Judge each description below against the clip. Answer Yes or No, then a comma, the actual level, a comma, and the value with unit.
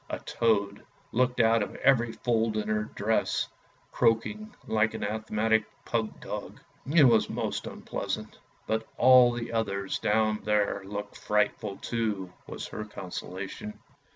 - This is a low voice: Yes, low, 110 Hz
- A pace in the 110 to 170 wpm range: Yes, average, 140 wpm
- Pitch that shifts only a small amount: Yes, narrow, 1.8 semitones